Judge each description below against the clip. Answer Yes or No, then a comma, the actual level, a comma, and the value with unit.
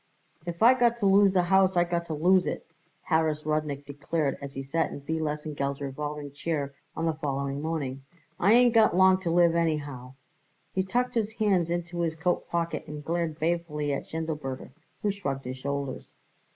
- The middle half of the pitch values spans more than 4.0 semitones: No, average, 3.7 semitones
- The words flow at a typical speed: Yes, average, 185 wpm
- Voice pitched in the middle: Yes, medium, 160 Hz